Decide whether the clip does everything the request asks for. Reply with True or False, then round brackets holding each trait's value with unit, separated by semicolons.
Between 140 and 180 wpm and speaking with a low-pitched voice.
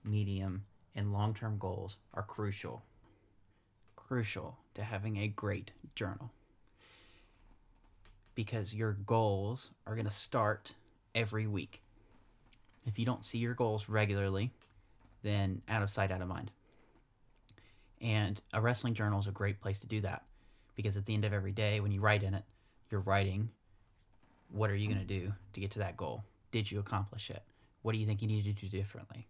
True (170 wpm; 105 Hz)